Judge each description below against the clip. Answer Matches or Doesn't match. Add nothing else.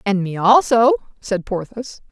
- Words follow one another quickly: Doesn't match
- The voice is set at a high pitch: Matches